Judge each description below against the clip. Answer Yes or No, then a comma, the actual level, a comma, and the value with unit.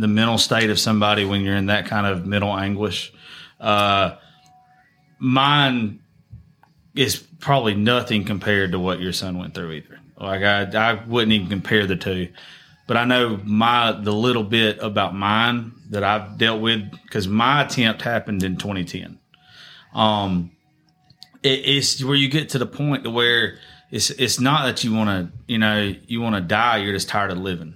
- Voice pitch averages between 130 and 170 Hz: No, low, 110 Hz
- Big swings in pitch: No, average, 3.5 semitones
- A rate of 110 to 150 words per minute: No, average, 175 wpm